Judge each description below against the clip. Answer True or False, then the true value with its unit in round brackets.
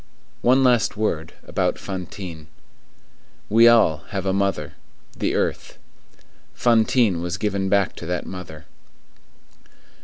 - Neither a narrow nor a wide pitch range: True (4.1 semitones)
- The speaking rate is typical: False (110 wpm)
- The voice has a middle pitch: False (95 Hz)